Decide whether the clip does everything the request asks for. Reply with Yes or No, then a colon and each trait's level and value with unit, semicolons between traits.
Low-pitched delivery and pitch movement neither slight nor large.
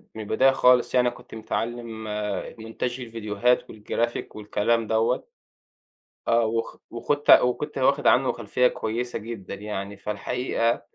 No: low, 115 Hz; narrow, 2.2 semitones